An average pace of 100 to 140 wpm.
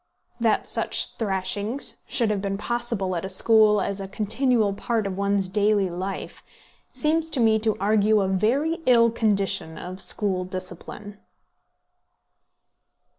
Yes: slow, 135 wpm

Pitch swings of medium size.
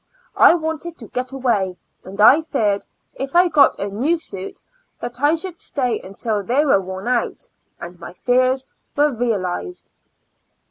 No: wide, 6.7 semitones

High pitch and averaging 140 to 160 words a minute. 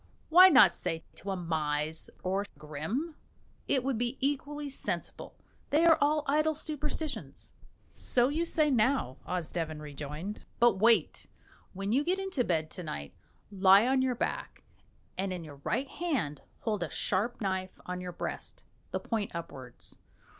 Yes: high, 205 Hz; average, 155 wpm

